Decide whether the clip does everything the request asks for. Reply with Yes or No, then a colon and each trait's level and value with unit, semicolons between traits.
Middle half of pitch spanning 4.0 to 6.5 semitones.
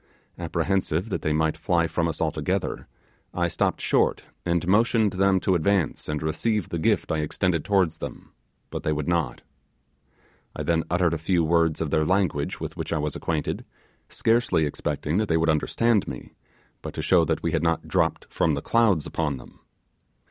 No: average, 3.3 semitones